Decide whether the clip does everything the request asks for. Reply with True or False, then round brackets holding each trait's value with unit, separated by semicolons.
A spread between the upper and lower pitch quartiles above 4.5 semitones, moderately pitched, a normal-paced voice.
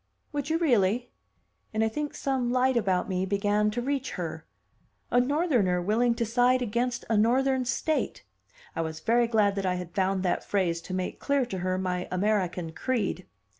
False (5.2 semitones; 220 Hz; 180 wpm)